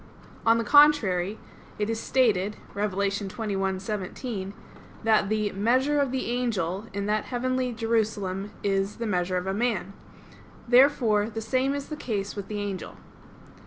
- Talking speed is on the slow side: No, average, 145 wpm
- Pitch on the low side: No, high, 215 Hz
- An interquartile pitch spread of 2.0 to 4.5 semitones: Yes, average, 3.7 semitones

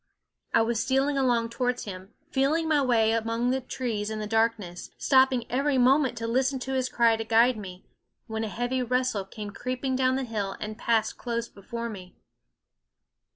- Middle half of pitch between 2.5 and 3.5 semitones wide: Yes, average, 2.8 semitones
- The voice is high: Yes, high, 235 Hz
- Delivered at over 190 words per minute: No, average, 180 wpm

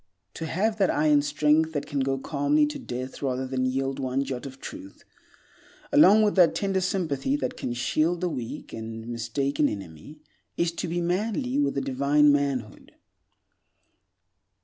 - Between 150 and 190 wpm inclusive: Yes, average, 160 wpm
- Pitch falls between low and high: Yes, medium, 145 Hz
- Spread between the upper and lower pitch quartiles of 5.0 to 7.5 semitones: Yes, wide, 5.6 semitones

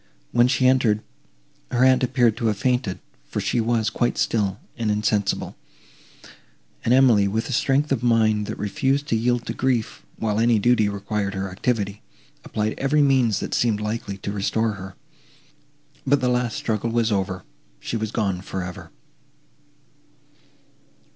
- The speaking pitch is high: No, low, 110 Hz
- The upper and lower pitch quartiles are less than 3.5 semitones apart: Yes, average, 3.1 semitones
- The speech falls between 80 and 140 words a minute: No, average, 155 wpm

